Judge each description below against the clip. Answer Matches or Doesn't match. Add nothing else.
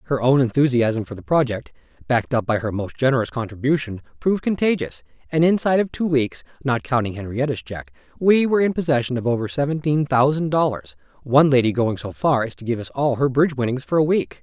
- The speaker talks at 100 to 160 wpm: Doesn't match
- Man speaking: Matches